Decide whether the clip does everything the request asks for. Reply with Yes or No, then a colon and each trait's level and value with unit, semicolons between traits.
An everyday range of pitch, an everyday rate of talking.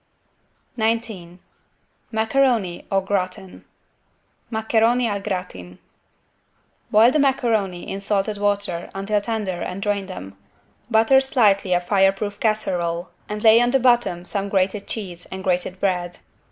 No: average, 3.2 semitones; slow, 125 wpm